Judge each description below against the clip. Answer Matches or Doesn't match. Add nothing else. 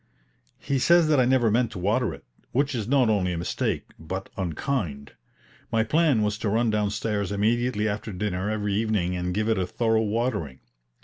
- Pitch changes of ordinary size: Matches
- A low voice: Matches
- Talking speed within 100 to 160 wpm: Doesn't match